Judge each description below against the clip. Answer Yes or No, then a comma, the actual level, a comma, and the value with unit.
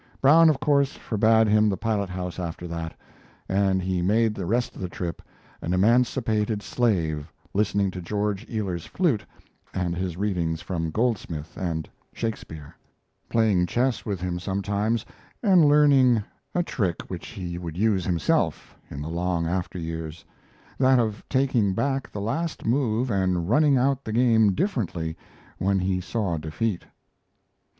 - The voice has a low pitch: Yes, low, 100 Hz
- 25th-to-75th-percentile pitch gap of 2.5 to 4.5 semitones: No, average, 4.9 semitones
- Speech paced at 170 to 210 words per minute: No, average, 145 wpm